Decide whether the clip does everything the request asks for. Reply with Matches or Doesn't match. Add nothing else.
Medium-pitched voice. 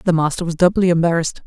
Matches